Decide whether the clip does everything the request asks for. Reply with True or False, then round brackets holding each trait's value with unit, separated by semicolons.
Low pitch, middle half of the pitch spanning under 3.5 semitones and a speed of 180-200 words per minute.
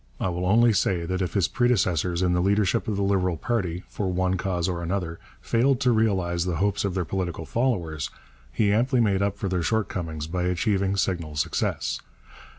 True (95 Hz; 2.8 semitones; 190 wpm)